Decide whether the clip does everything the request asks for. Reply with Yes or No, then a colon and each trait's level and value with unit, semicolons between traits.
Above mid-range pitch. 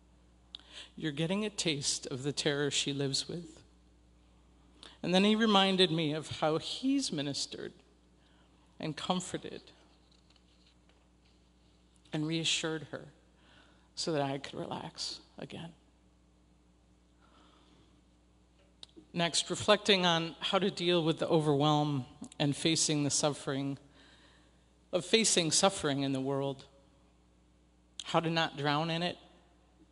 No: medium, 140 Hz